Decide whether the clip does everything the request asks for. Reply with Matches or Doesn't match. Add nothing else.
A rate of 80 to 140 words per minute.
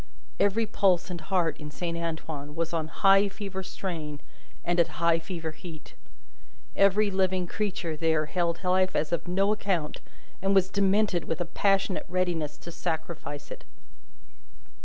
Doesn't match